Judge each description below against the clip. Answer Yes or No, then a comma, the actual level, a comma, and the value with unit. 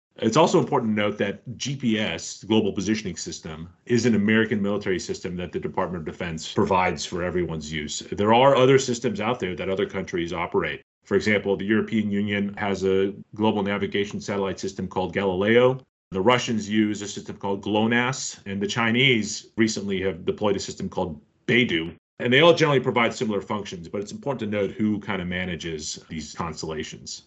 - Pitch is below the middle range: Yes, low, 105 Hz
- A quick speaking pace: No, average, 185 wpm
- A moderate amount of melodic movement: Yes, average, 3.1 semitones